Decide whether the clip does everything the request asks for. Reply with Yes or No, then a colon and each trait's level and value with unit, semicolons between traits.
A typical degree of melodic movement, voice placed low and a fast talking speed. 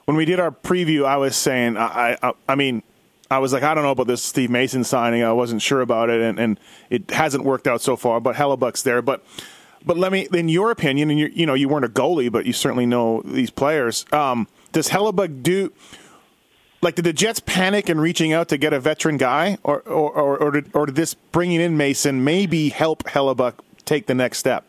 No: average, 4.4 semitones; medium, 145 Hz; fast, 230 wpm